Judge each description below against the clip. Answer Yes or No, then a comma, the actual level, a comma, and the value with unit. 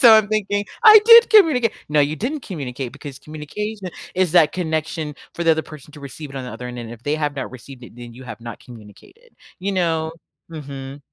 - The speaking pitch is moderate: Yes, medium, 155 Hz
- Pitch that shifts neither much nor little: No, wide, 6.9 semitones